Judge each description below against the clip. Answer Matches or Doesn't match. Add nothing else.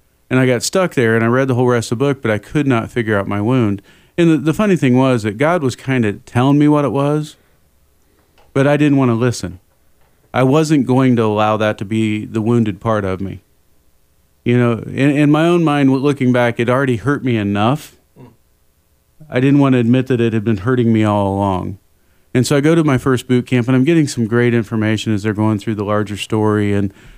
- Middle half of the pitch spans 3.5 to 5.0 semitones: Matches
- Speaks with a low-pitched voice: Matches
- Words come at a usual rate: Doesn't match